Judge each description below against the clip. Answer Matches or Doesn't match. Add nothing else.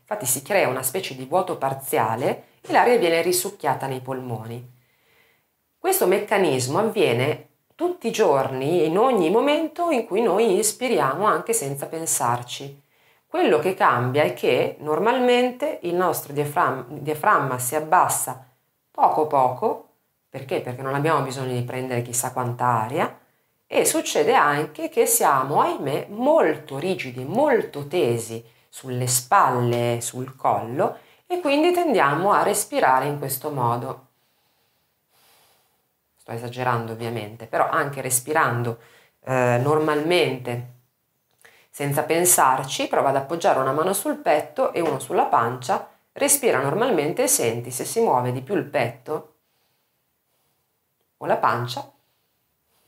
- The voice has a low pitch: Doesn't match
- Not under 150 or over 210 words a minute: Doesn't match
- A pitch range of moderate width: Doesn't match